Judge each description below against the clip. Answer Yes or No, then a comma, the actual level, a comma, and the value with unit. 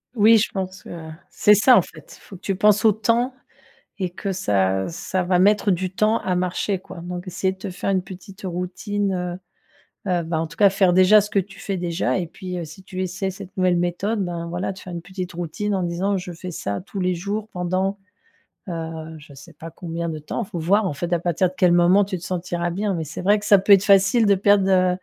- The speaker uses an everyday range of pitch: No, narrow, 2.3 semitones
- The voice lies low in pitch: No, medium, 185 Hz